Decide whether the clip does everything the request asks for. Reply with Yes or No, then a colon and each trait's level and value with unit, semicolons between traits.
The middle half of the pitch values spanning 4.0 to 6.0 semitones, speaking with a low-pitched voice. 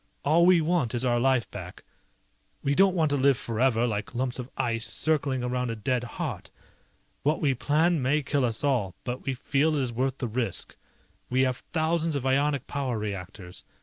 No: average, 3.4 semitones; low, 130 Hz